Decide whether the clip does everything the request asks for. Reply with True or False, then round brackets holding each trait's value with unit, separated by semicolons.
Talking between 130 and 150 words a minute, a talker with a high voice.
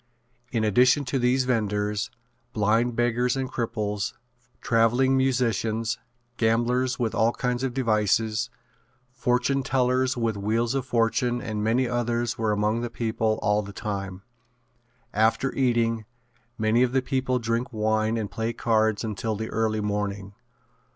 False (135 wpm; 115 Hz)